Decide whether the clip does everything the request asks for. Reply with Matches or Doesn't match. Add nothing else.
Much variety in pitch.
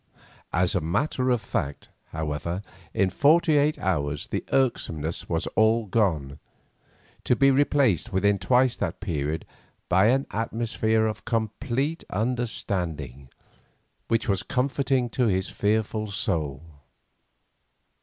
Matches